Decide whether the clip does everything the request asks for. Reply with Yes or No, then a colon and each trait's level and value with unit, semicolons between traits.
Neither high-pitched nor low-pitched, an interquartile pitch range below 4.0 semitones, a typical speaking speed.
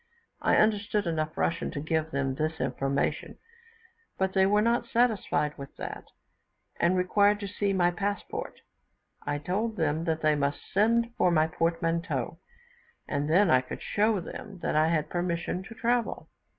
No: medium, 175 Hz; average, 4.8 semitones; average, 160 wpm